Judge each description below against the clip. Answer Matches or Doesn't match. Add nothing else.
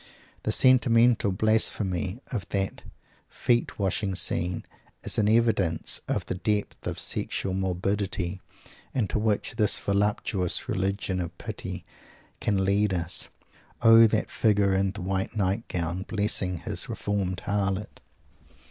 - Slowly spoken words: Matches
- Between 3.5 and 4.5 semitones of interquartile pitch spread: Doesn't match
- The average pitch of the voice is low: Matches